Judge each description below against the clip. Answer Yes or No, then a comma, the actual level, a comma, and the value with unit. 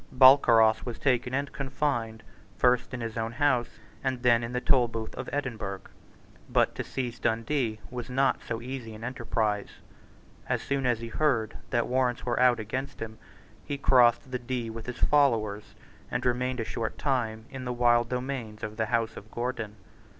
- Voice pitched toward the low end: Yes, low, 120 Hz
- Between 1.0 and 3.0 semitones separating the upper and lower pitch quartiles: Yes, narrow, 2.4 semitones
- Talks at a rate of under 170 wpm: No, average, 175 wpm